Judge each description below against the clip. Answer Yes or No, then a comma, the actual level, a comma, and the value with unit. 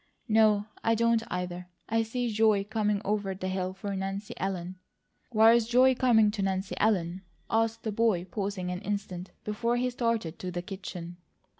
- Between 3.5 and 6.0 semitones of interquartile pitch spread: No, average, 3.1 semitones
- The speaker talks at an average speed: Yes, average, 170 wpm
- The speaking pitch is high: Yes, high, 205 Hz